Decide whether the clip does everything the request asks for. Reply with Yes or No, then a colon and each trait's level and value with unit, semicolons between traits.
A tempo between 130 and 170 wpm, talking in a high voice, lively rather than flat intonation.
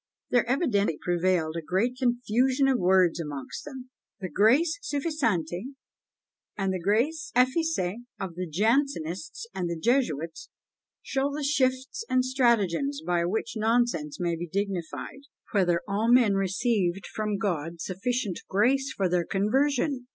Yes: slow, 135 wpm; high, 210 Hz; wide, 6.5 semitones